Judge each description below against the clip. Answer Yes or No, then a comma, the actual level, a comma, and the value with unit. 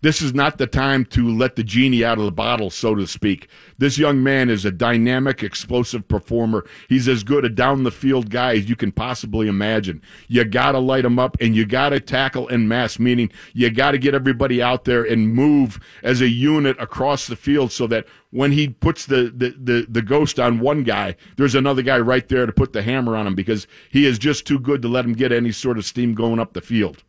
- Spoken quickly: Yes, fast, 230 wpm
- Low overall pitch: Yes, low, 125 Hz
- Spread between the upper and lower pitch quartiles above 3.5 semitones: No, average, 2.8 semitones